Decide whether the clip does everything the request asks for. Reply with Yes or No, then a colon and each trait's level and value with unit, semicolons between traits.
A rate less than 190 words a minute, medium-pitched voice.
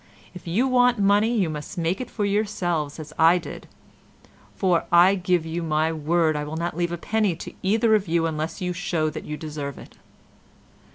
No: average, 195 wpm; medium, 175 Hz